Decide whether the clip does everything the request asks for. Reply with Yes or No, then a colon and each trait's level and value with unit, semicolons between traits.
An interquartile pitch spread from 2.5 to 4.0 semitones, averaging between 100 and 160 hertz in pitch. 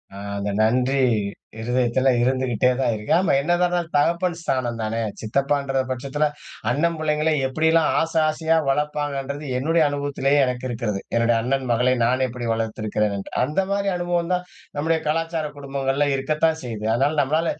No: average, 4.4 semitones; medium, 140 Hz